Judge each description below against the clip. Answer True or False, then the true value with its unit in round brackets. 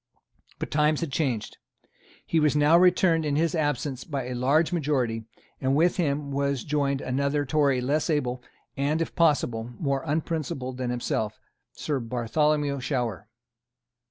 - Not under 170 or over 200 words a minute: False (145 wpm)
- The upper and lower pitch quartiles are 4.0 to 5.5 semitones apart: False (3.2 semitones)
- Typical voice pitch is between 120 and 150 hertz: True (140 Hz)